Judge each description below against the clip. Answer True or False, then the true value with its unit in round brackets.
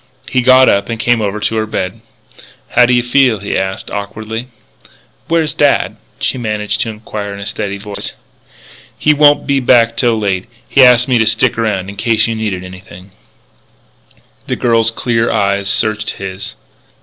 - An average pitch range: True (3.2 semitones)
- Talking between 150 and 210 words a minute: True (180 wpm)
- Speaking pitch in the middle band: False (110 Hz)